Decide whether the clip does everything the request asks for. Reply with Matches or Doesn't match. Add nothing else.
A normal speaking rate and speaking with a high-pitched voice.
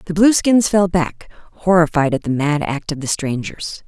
Doesn't match